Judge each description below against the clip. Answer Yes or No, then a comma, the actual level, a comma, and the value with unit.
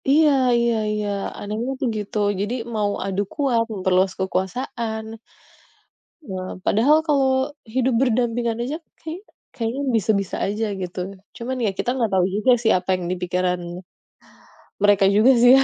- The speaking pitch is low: No, high, 220 Hz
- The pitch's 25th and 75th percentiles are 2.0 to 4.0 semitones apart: No, average, 4.5 semitones